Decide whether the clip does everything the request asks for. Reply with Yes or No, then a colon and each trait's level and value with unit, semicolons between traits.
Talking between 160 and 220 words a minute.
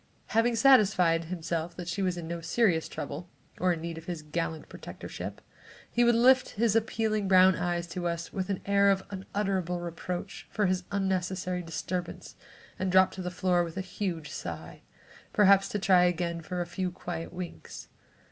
Yes: average, 175 wpm